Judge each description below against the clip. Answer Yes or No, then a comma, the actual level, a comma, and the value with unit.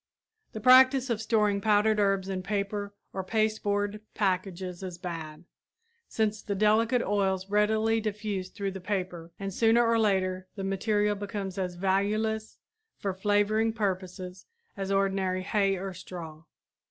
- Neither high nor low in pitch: No, high, 200 Hz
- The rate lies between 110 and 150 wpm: Yes, average, 140 wpm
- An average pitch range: No, narrow, 2.3 semitones